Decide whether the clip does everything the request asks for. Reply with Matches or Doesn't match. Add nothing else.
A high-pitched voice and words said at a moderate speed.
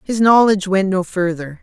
Matches